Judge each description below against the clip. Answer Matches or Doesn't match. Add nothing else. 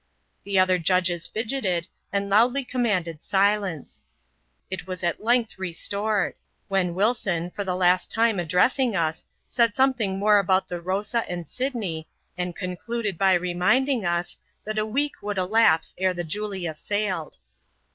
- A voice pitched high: Matches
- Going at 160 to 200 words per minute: Doesn't match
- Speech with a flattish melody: Doesn't match